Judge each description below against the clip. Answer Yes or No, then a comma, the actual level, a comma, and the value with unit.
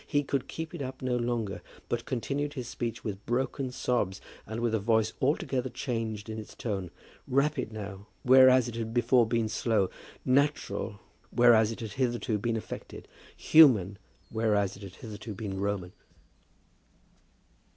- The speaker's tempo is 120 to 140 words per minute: No, average, 150 wpm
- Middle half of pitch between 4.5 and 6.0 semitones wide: No, average, 3.4 semitones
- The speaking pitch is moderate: No, low, 115 Hz